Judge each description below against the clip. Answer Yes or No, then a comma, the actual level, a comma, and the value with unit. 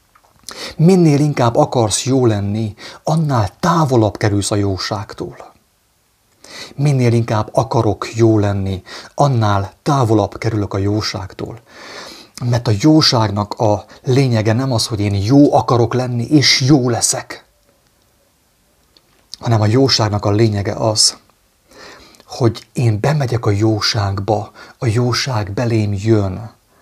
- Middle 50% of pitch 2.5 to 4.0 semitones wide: Yes, average, 3.5 semitones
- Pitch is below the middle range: Yes, low, 115 Hz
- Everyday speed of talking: No, slow, 110 wpm